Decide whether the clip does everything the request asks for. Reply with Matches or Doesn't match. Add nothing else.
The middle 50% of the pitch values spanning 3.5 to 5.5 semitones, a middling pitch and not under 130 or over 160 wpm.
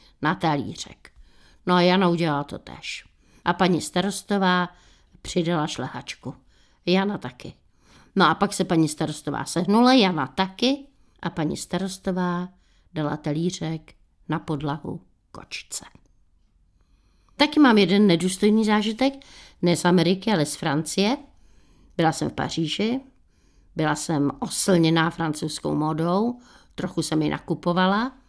Doesn't match